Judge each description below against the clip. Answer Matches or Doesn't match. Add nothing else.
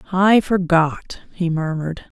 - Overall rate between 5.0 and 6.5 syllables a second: Doesn't match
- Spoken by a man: Doesn't match